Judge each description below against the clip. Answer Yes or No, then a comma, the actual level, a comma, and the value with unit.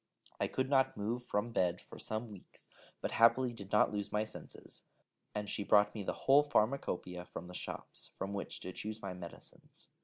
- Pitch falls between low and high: No, low, 105 Hz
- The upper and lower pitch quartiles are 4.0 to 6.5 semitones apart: No, average, 3.3 semitones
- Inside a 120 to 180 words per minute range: No, average, 190 wpm